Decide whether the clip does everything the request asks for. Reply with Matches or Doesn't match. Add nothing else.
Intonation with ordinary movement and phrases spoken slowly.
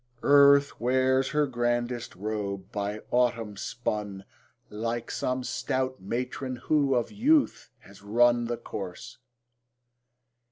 Matches